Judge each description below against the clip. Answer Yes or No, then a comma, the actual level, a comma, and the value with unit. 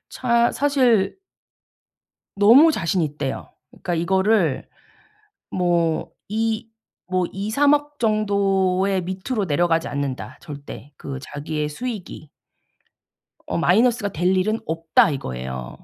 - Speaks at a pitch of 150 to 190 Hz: Yes, medium, 185 Hz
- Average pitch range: No, wide, 5.7 semitones